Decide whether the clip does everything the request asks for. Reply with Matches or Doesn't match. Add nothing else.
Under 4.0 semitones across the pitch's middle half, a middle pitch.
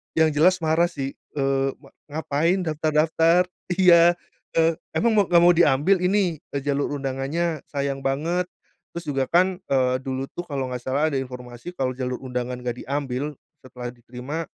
Doesn't match